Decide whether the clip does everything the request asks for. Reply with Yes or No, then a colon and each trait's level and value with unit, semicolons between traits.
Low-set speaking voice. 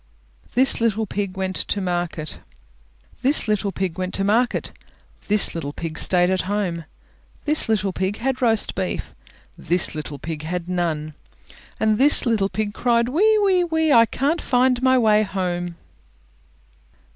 No: high, 205 Hz